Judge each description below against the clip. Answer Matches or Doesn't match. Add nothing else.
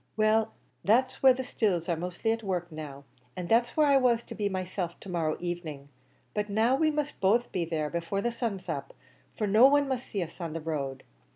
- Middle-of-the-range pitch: Doesn't match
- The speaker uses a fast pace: Matches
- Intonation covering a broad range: Matches